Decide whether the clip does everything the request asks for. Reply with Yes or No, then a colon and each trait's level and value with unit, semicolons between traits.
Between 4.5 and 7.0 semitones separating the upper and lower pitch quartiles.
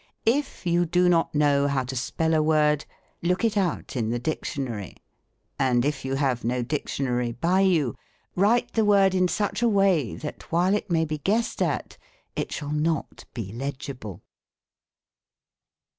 Yes: wide, 5.6 semitones